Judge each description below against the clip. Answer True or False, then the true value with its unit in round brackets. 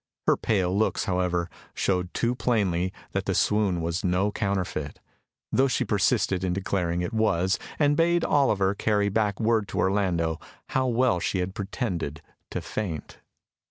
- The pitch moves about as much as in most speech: True (3.6 semitones)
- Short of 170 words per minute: True (155 wpm)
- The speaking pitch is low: True (95 Hz)